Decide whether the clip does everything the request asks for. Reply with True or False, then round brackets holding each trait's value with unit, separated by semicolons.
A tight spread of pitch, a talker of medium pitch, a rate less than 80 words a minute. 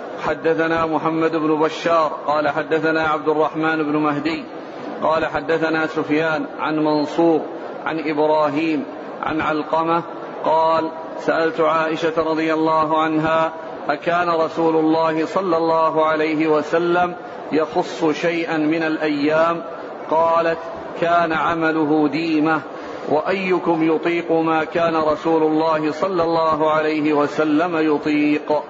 False (0.9 semitones; 160 Hz; 105 wpm)